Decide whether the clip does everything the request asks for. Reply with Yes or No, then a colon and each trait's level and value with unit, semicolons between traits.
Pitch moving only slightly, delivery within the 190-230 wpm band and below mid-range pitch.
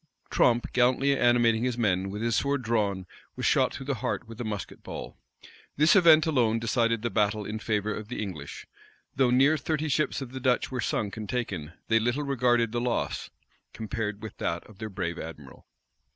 No: average, 3.2 semitones; average, 195 wpm; low, 115 Hz